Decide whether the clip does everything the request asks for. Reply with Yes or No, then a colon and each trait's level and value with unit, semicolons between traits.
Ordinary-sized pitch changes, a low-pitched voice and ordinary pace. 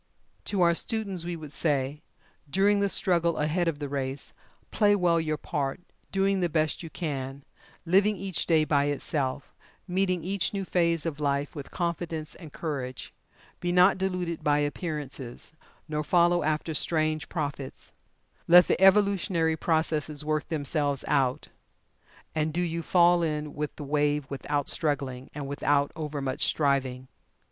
No: average, 3.4 semitones; medium, 155 Hz; average, 150 wpm